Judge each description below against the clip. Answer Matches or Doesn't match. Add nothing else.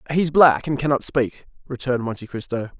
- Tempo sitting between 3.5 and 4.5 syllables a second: Doesn't match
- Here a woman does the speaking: Doesn't match